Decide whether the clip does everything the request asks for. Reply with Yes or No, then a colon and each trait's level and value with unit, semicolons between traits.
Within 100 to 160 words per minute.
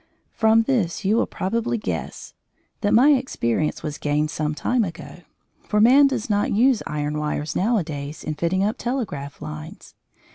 Yes: average, 155 wpm